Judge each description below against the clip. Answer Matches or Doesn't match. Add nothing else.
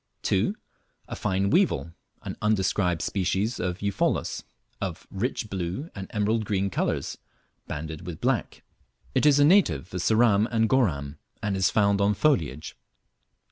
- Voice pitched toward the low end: Matches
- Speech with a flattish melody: Doesn't match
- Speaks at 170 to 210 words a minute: Doesn't match